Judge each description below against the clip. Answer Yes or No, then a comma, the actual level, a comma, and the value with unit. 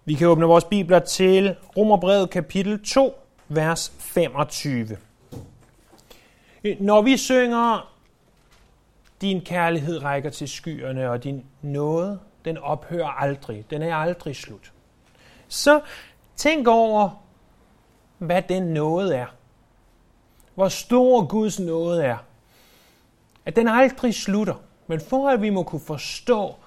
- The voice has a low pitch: No, medium, 170 Hz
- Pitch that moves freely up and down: Yes, wide, 6.7 semitones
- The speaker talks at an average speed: No, slow, 115 wpm